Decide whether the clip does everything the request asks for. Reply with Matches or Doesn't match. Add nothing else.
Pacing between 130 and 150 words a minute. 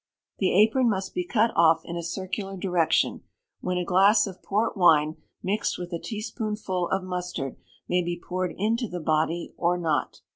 Doesn't match